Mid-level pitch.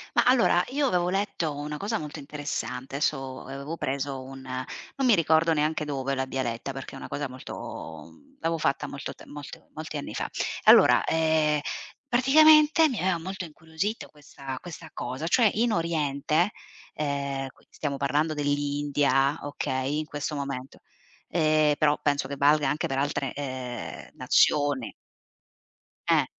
Yes: medium, 145 Hz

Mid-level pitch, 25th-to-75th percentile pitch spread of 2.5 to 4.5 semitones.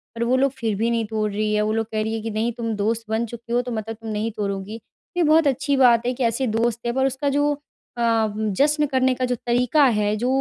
No: high, 230 Hz; average, 2.8 semitones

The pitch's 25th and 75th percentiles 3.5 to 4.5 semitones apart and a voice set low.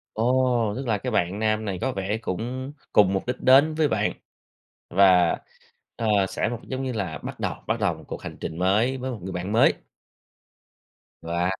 No: average, 5.2 semitones; low, 110 Hz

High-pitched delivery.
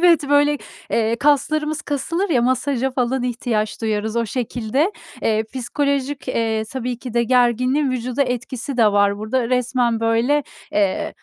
Yes: very high, 250 Hz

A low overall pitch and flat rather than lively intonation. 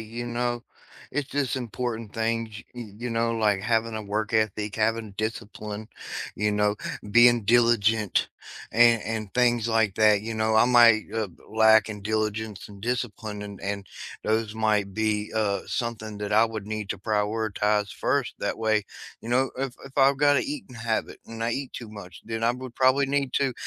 Yes: low, 110 Hz; narrow, 2.1 semitones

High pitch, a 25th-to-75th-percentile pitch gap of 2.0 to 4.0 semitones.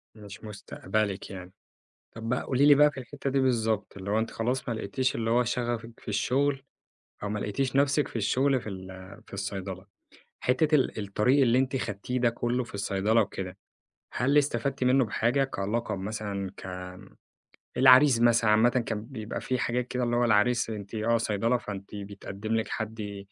No: low, 115 Hz; average, 3.6 semitones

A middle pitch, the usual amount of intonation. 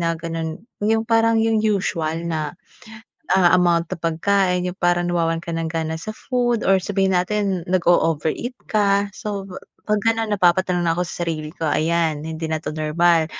Yes: medium, 175 Hz; average, 3.5 semitones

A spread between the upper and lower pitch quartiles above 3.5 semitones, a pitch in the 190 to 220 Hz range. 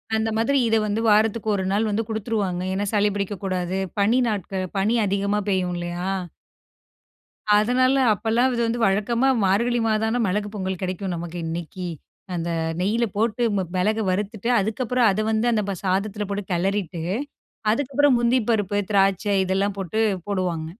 No: average, 2.9 semitones; high, 205 Hz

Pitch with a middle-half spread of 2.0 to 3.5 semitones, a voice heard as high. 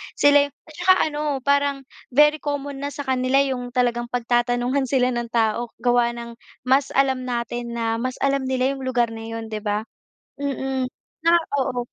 Yes: narrow, 2.6 semitones; very high, 255 Hz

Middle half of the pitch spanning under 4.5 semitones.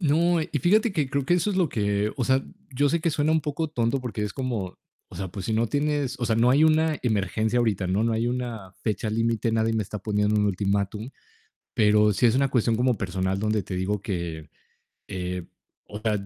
No: average, 5.1 semitones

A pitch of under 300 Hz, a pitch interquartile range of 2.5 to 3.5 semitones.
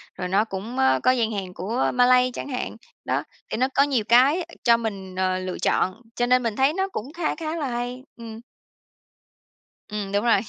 No: high, 235 Hz; average, 4.4 semitones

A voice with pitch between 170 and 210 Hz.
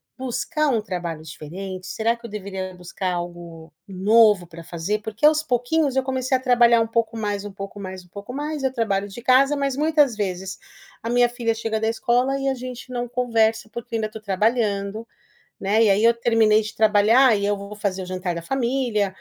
No: high, 220 Hz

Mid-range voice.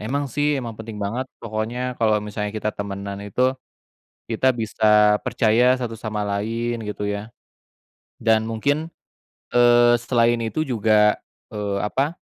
No: low, 115 Hz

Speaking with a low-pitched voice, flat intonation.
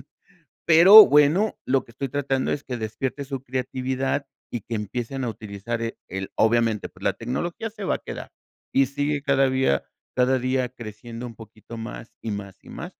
No: low, 125 Hz; average, 3.3 semitones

